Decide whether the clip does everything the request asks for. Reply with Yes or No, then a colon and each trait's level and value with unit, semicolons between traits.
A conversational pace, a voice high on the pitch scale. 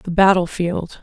No: average, 175 wpm; medium, 180 Hz